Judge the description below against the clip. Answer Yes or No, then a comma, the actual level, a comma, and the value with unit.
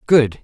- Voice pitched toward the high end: No, low, 135 Hz